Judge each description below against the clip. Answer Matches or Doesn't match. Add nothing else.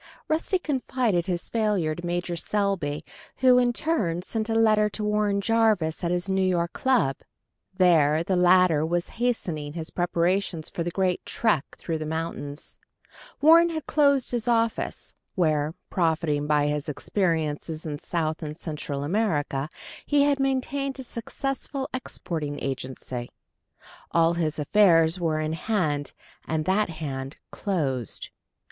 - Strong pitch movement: Matches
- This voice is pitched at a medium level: Matches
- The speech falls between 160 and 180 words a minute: Doesn't match